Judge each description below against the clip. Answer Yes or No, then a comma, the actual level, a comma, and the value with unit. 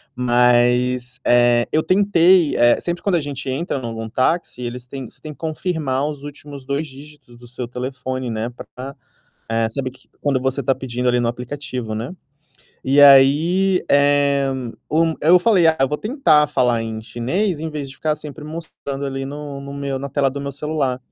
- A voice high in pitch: No, medium, 140 Hz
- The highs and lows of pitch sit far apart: No, average, 3.4 semitones